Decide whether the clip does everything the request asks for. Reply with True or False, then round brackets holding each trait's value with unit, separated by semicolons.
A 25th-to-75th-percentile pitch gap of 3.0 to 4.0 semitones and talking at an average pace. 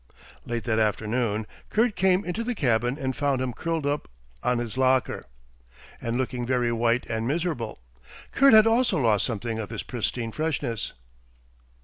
False (5.2 semitones; 155 wpm)